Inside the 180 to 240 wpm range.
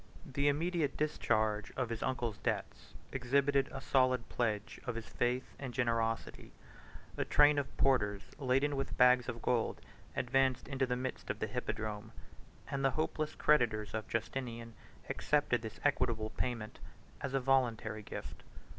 No: average, 145 wpm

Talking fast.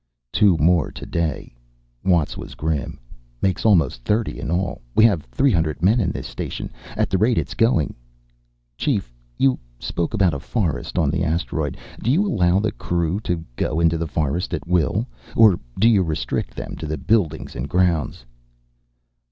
No: average, 175 wpm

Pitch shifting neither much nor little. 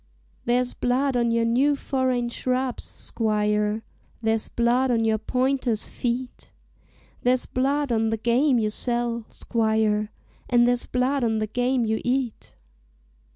No: narrow, 2.3 semitones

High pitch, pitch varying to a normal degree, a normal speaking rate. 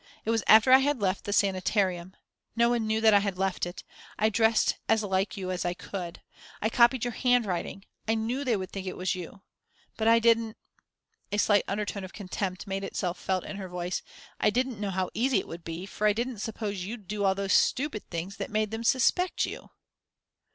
No: high, 205 Hz; average, 3.2 semitones; fast, 215 wpm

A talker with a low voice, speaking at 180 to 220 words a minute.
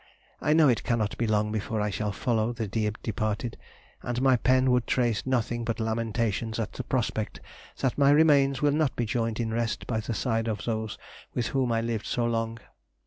Yes: low, 115 Hz; average, 200 wpm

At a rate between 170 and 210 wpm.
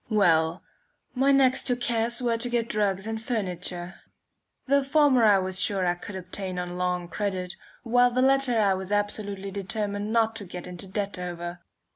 Yes: average, 180 wpm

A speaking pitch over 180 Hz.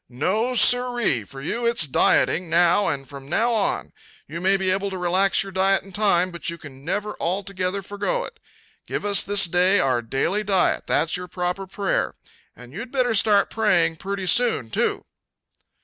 Yes: high, 190 Hz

